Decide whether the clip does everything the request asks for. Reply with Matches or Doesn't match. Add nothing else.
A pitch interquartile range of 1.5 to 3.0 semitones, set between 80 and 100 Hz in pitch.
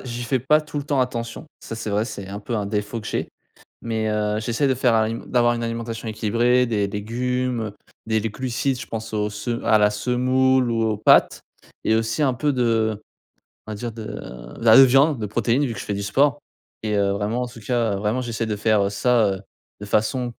Doesn't match